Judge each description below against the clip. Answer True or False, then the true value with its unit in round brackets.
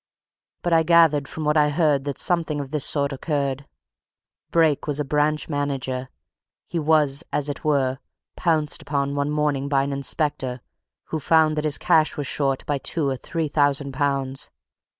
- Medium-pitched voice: True (145 Hz)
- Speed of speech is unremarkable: True (170 wpm)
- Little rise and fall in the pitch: True (1.8 semitones)